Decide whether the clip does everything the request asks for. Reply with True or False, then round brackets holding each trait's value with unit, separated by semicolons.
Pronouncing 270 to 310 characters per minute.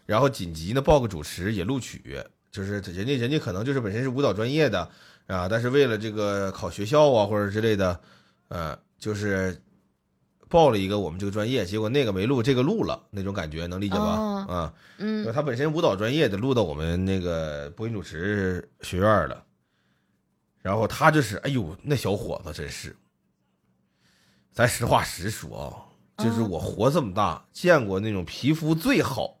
True (275 characters per minute)